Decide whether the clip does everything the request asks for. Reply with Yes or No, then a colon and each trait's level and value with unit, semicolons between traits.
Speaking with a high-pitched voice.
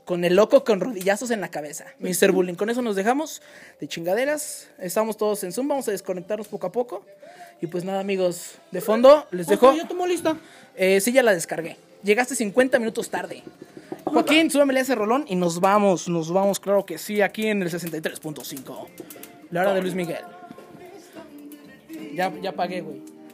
Yes: high, 200 Hz